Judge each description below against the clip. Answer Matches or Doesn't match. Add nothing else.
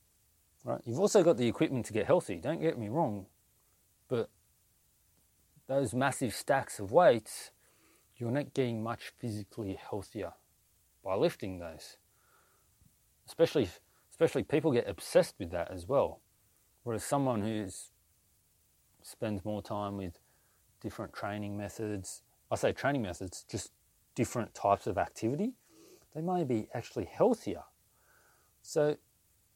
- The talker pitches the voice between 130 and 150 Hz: Doesn't match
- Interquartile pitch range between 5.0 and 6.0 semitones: Matches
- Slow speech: Matches